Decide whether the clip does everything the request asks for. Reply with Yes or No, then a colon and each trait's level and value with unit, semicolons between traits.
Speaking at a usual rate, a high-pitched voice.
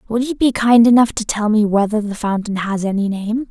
No: fast, 240 wpm; high, 220 Hz